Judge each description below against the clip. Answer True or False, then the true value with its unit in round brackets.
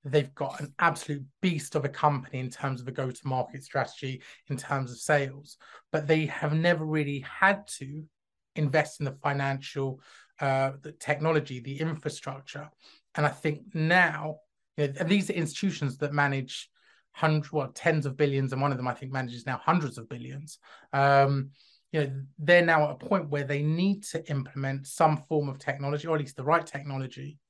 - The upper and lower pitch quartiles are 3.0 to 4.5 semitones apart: False (2.4 semitones)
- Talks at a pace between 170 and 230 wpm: True (185 wpm)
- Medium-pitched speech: True (145 Hz)